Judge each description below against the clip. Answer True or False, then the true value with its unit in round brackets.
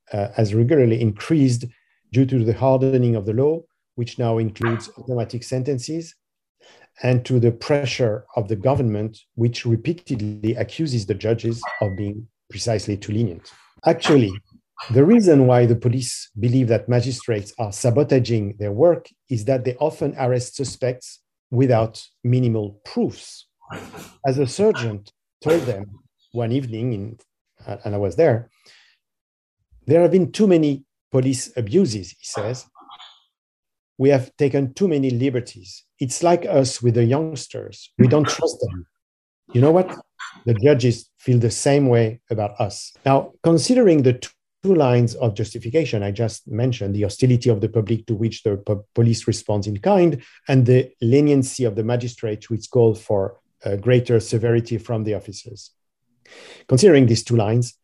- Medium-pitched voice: False (120 Hz)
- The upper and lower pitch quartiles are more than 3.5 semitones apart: False (3.1 semitones)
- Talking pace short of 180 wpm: True (150 wpm)